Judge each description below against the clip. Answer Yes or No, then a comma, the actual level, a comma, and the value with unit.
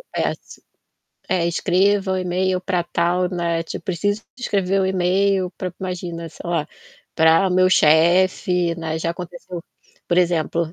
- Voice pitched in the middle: Yes, medium, 180 Hz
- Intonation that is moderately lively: No, narrow, 1.7 semitones